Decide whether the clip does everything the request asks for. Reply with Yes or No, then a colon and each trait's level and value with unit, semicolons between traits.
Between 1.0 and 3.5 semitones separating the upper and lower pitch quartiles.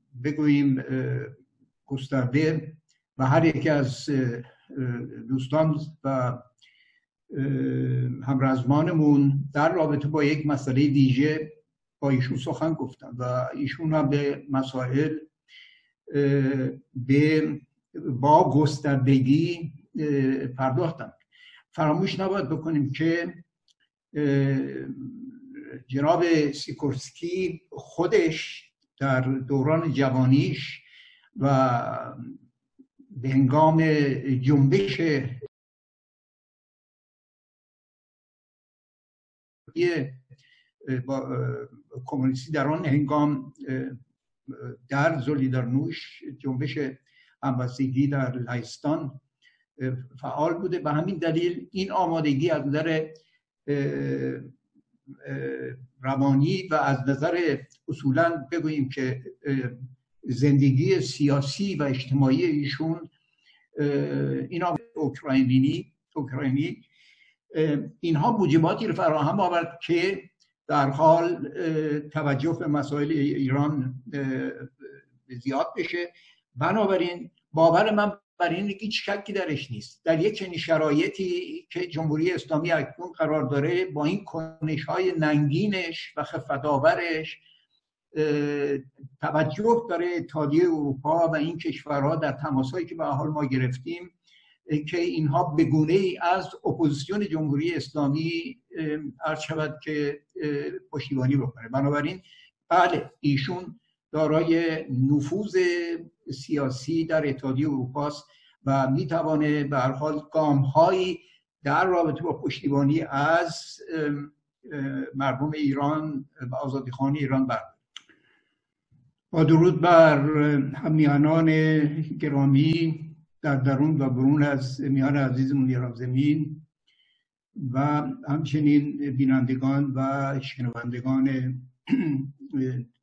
Yes: average, 3.2 semitones